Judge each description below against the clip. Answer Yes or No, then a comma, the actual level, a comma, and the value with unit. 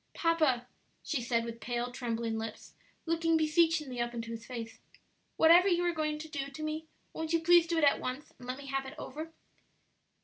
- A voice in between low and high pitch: No, very high, 285 Hz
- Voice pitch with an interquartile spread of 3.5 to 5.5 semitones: Yes, average, 5.1 semitones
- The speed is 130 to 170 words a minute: No, average, 200 wpm